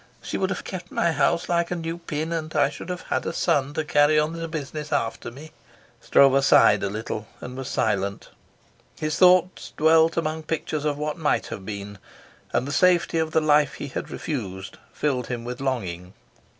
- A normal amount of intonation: Yes, average, 4.6 semitones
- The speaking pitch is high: No, medium, 150 Hz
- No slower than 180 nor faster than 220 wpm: Yes, average, 195 wpm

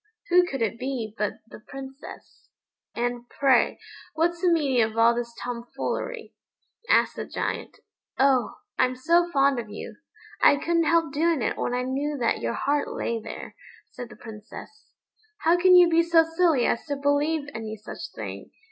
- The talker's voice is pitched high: Yes, very high, 275 Hz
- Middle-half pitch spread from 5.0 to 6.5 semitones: Yes, wide, 5.6 semitones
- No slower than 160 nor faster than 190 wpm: Yes, average, 170 wpm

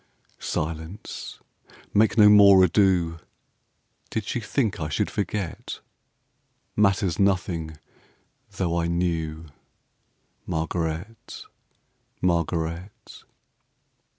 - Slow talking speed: Yes, slow, 75 wpm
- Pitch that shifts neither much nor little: Yes, average, 3.5 semitones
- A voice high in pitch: No, very low, 90 Hz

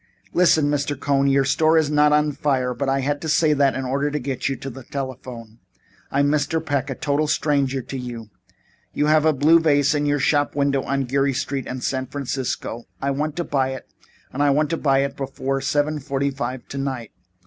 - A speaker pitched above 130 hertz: Yes, medium, 140 Hz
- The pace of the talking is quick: Yes, fast, 215 wpm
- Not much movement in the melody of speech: Yes, narrow, 1.7 semitones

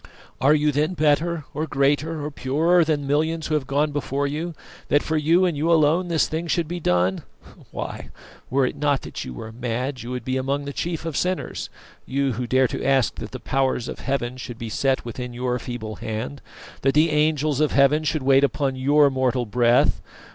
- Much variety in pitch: No, average, 3.2 semitones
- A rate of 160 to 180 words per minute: No, fast, 205 wpm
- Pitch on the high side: No, medium, 140 Hz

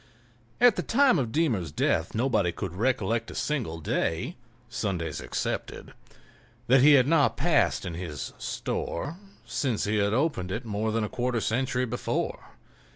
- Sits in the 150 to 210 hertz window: No, low, 115 Hz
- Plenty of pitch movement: Yes, wide, 5.8 semitones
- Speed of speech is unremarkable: Yes, average, 155 wpm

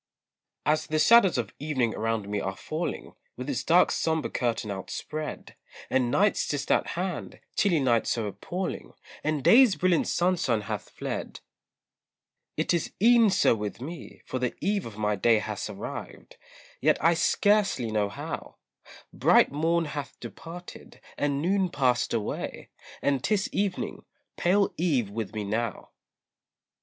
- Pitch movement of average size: No, wide, 7.5 semitones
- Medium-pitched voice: Yes, medium, 145 Hz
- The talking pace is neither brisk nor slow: Yes, average, 145 wpm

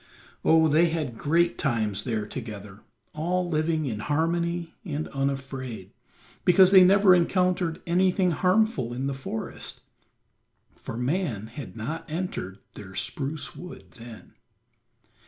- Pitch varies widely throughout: Yes, wide, 6.4 semitones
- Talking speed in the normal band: No, slow, 120 wpm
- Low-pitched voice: No, medium, 155 Hz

